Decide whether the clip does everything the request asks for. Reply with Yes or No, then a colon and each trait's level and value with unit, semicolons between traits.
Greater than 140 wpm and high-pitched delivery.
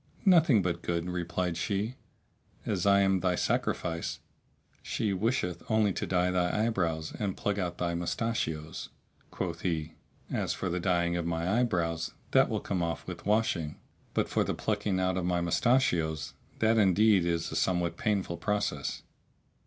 No: average, 160 wpm; very low, 90 Hz